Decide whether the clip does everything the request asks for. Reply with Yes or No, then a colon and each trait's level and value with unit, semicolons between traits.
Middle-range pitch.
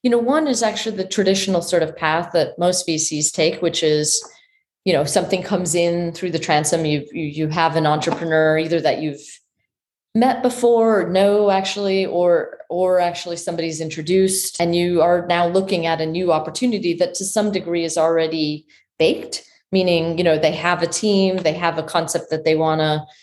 Yes: medium, 170 Hz